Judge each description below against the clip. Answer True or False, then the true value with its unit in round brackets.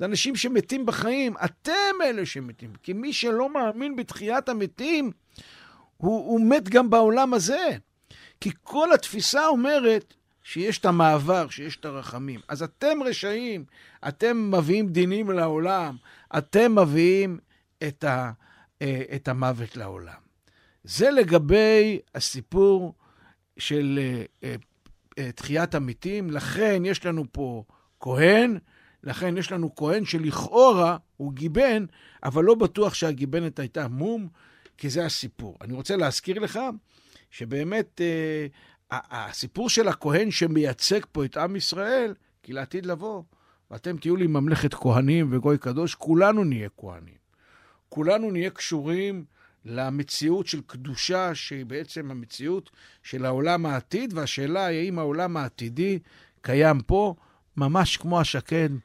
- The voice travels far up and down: True (6.6 semitones)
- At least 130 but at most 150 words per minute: False (120 wpm)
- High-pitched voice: False (165 Hz)